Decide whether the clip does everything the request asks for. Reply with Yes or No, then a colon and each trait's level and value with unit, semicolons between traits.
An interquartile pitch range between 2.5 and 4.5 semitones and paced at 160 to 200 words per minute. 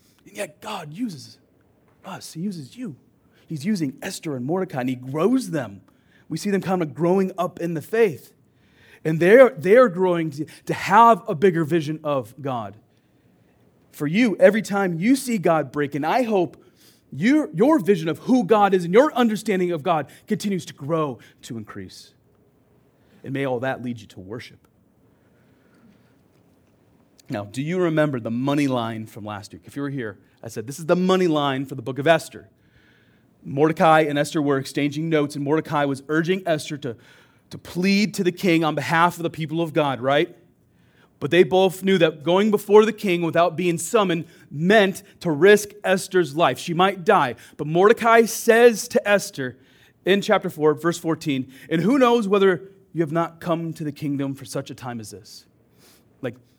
No: wide, 5.6 semitones; average, 180 wpm